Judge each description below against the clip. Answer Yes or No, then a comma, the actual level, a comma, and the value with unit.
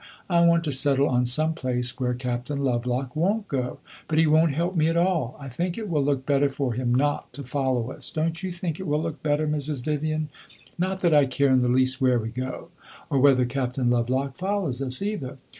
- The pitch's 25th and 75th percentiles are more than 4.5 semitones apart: No, average, 3.9 semitones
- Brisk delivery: Yes, fast, 220 wpm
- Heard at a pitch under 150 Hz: Yes, medium, 140 Hz